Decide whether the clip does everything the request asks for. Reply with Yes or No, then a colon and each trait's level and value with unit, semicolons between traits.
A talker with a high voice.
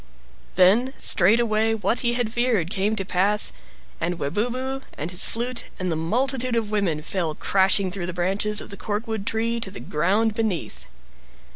Yes: high, 210 Hz